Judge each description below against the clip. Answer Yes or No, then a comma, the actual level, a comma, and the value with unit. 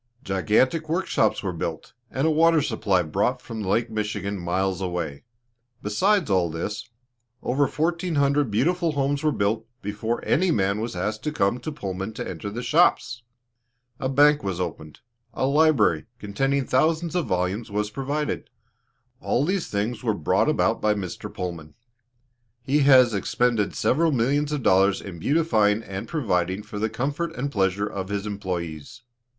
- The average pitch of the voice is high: No, low, 110 Hz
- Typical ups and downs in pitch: No, wide, 6.7 semitones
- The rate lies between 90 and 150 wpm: No, average, 160 wpm